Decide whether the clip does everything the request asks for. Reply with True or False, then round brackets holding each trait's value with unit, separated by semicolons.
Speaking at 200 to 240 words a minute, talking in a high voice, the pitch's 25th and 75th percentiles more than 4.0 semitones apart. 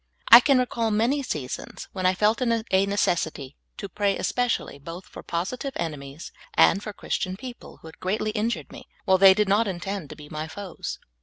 True (205 wpm; 195 Hz; 4.8 semitones)